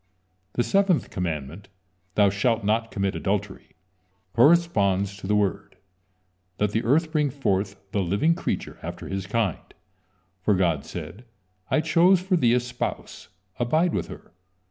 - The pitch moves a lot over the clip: Yes, wide, 7.1 semitones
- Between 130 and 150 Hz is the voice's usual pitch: No, low, 105 Hz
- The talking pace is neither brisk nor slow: Yes, average, 145 wpm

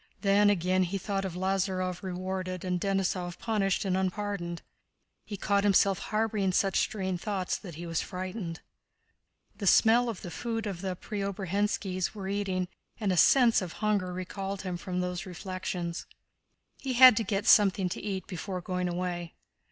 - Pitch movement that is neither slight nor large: No, narrow, 2.1 semitones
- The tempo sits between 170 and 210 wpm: No, average, 160 wpm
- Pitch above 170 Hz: Yes, high, 190 Hz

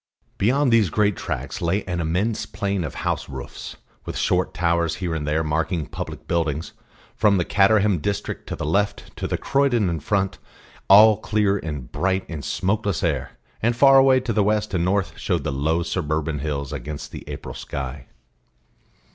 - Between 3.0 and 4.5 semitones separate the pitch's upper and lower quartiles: No, average, 4.9 semitones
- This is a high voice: No, very low, 90 Hz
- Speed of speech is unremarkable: Yes, average, 170 wpm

